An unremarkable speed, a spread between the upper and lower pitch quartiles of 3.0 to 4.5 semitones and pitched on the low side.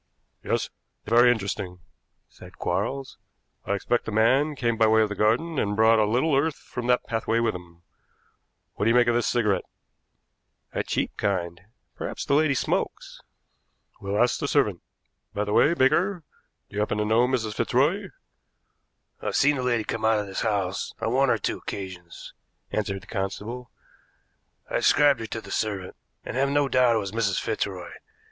Yes: average, 180 wpm; average, 3.9 semitones; low, 115 Hz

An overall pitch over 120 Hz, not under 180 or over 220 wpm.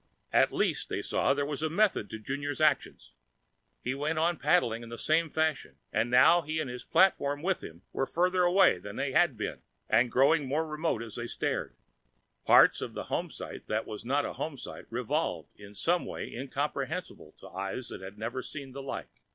Yes: medium, 140 Hz; average, 190 wpm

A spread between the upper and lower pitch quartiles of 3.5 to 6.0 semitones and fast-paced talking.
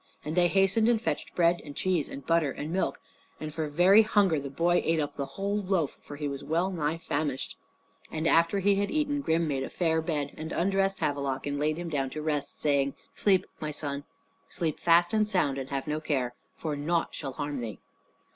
Yes: average, 4.1 semitones; fast, 215 wpm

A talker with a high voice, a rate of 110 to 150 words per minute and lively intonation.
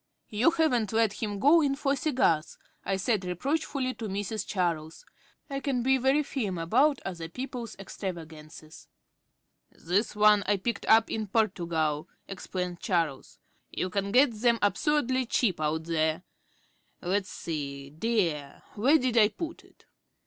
Yes: high, 205 Hz; average, 145 wpm; wide, 6.8 semitones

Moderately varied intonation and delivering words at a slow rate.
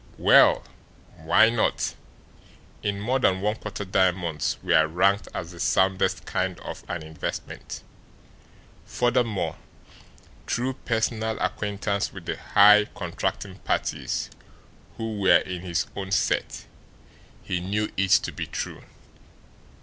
Yes: average, 3.1 semitones; slow, 120 wpm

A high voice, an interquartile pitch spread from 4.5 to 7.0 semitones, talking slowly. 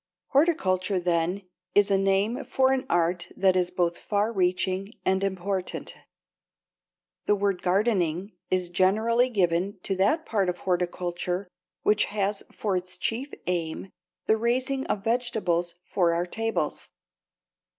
No: high, 195 Hz; average, 3.3 semitones; slow, 130 wpm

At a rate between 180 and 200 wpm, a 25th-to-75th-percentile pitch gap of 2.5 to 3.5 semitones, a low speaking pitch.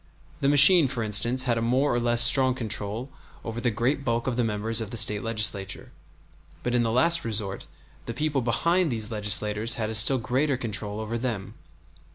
Yes: average, 195 wpm; average, 3.0 semitones; low, 115 Hz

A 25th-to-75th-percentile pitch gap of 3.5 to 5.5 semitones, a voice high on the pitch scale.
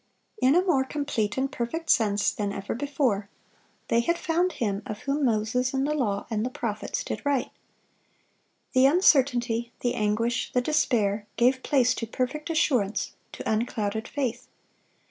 Yes: average, 4.4 semitones; high, 245 Hz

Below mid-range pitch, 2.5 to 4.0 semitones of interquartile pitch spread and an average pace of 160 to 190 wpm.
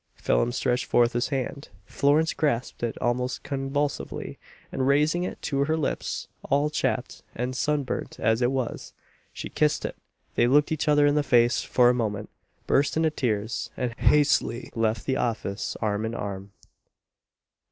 Yes: low, 130 Hz; average, 3.6 semitones; average, 165 wpm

